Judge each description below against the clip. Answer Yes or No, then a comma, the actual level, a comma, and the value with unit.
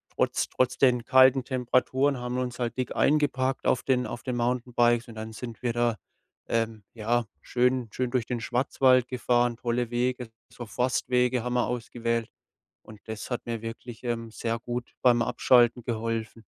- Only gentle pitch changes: Yes, narrow, 1.4 semitones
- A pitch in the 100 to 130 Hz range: Yes, low, 120 Hz